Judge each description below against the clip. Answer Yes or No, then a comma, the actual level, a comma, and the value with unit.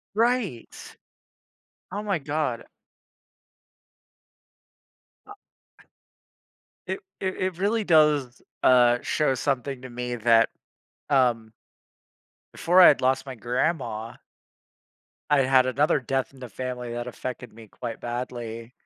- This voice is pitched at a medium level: No, low, 130 Hz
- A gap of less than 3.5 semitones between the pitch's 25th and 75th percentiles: No, average, 4.0 semitones